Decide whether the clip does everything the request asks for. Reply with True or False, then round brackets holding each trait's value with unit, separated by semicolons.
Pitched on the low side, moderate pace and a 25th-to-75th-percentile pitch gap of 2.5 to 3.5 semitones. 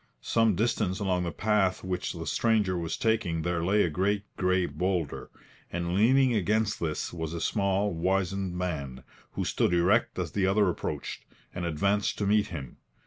True (95 Hz; 170 wpm; 3.1 semitones)